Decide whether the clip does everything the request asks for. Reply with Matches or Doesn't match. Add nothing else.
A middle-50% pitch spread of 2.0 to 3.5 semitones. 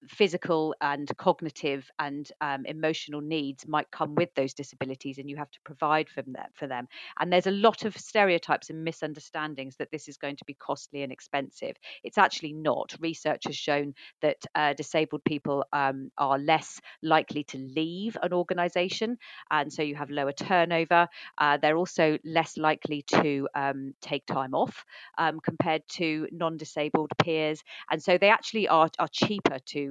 Matches